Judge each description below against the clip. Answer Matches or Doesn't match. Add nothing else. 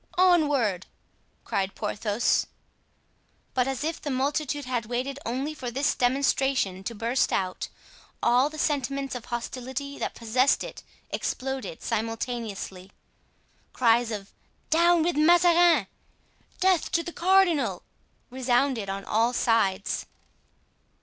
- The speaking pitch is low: Doesn't match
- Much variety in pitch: Doesn't match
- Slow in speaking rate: Matches